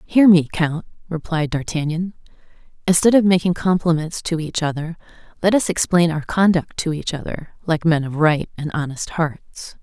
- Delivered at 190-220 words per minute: No, average, 165 wpm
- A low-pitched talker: No, medium, 165 Hz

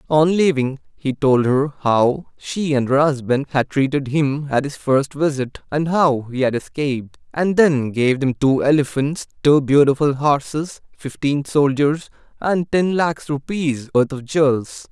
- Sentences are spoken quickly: No, average, 160 wpm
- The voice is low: No, medium, 145 Hz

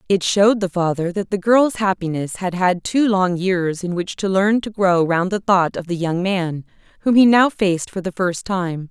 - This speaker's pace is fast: Yes, fast, 230 wpm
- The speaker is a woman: Yes, female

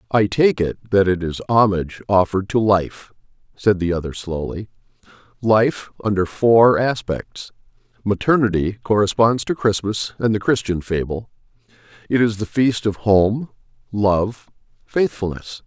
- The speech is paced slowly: Yes, slow, 125 wpm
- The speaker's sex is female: No, male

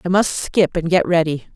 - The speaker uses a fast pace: Yes, fast, 230 wpm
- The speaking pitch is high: No, medium, 170 Hz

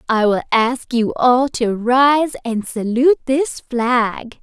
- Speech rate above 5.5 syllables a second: No, 4.4 syllables/s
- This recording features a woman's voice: Yes, female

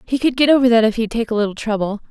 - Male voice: No, female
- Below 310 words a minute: No, fast, 315 wpm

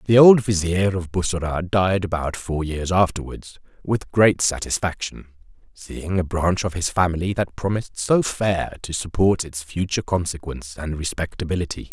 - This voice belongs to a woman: No, male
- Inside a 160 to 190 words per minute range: No, average, 150 wpm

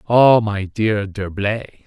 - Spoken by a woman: No, male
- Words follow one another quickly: No, slow, 130 wpm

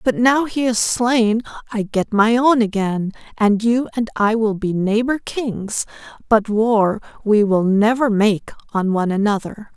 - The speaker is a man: No, female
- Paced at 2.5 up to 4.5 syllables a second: Yes, 4.0 syllables/s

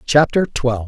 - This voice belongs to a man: Yes, male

